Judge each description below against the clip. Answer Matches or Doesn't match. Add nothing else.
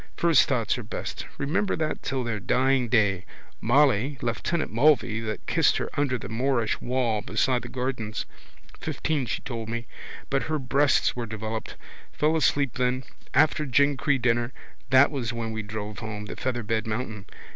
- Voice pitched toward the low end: Matches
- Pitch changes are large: Doesn't match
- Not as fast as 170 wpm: Matches